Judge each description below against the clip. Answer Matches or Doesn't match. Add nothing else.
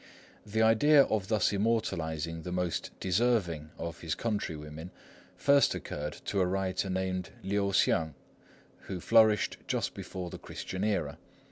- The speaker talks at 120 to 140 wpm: Matches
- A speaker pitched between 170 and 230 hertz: Doesn't match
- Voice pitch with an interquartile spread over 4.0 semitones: Matches